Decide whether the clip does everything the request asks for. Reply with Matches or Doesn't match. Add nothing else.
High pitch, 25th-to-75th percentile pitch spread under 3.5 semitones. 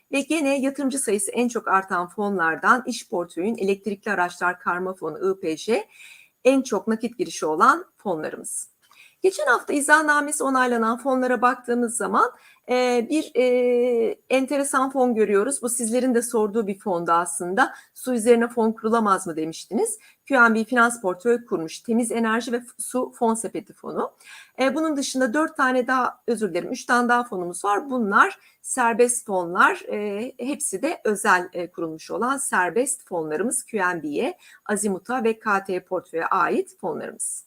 Doesn't match